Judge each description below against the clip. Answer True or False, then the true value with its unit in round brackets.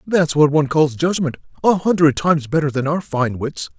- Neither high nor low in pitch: True (150 Hz)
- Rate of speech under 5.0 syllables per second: False (5.4 syllables/s)